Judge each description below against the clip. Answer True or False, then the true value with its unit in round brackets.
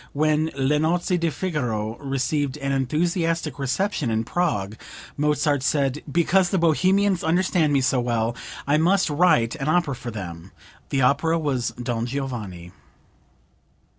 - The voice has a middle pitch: True (145 Hz)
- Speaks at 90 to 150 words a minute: True (135 wpm)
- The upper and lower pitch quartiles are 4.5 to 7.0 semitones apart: True (5.1 semitones)